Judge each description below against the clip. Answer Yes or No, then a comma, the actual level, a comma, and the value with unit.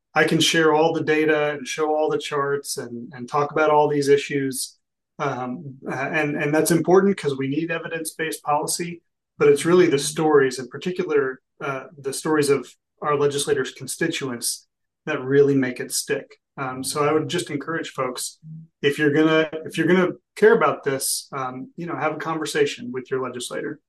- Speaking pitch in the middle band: Yes, medium, 155 Hz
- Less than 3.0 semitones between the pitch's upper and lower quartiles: Yes, narrow, 2.4 semitones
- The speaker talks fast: No, average, 180 wpm